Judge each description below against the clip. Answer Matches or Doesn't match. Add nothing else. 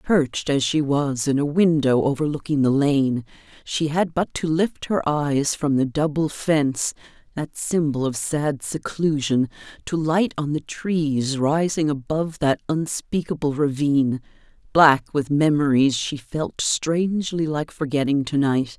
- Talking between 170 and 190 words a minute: Doesn't match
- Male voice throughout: Doesn't match